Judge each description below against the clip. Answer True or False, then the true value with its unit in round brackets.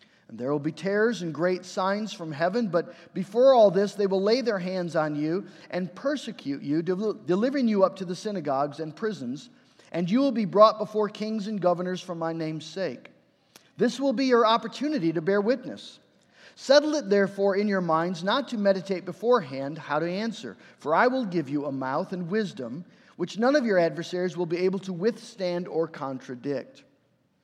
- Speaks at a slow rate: False (190 wpm)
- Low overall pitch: False (190 Hz)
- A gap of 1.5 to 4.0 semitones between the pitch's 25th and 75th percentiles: False (4.7 semitones)